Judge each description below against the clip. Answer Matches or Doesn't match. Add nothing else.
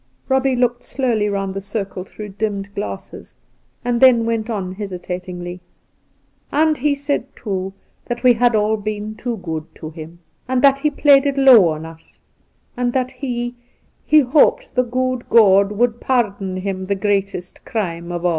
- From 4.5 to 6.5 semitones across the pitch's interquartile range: Matches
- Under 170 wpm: Doesn't match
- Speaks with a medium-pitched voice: Doesn't match